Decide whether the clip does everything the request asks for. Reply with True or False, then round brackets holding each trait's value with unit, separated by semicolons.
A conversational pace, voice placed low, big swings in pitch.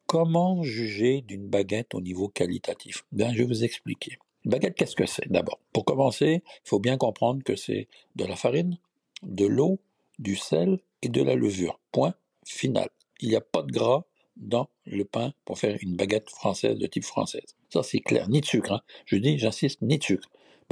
True (200 wpm; 120 Hz; 7.6 semitones)